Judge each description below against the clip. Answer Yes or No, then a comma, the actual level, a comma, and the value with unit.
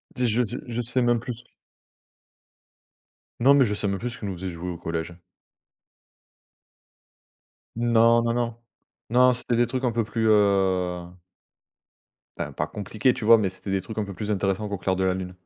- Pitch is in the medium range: No, low, 110 Hz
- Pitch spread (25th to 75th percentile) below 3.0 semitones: No, average, 3.8 semitones